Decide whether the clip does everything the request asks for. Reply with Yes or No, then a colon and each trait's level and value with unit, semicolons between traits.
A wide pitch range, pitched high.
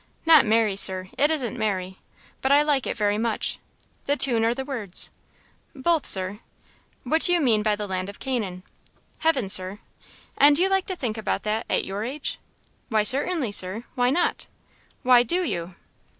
Yes: wide, 5.8 semitones; high, 235 Hz